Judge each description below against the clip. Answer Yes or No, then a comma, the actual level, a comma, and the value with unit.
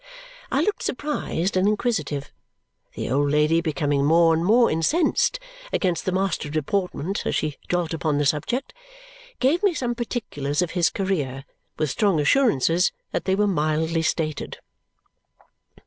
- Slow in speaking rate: No, average, 145 wpm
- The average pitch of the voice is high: No, medium, 165 Hz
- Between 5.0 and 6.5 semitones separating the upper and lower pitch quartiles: Yes, average, 5.3 semitones